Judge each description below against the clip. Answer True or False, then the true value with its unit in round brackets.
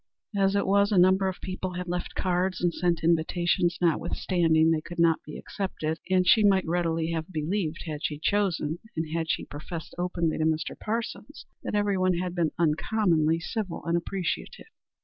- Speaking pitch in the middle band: True (175 Hz)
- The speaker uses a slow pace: False (175 wpm)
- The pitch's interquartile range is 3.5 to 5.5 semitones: False (2.6 semitones)